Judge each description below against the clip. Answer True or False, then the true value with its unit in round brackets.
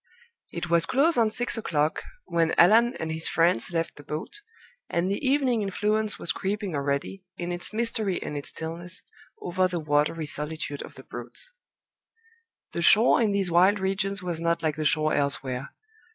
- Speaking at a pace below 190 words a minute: True (170 wpm)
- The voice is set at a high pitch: False (175 Hz)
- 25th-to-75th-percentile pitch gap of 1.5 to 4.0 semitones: False (4.7 semitones)